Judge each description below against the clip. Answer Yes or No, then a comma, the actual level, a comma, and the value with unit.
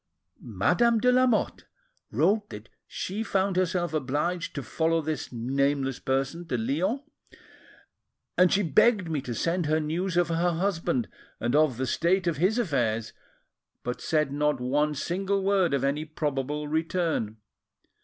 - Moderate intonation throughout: Yes, average, 5.0 semitones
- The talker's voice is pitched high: No, medium, 160 Hz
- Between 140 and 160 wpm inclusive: Yes, average, 145 wpm